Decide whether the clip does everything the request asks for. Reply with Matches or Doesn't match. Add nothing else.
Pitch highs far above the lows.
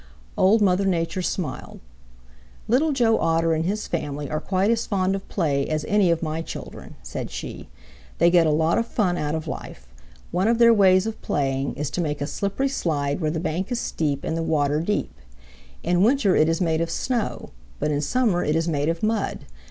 Doesn't match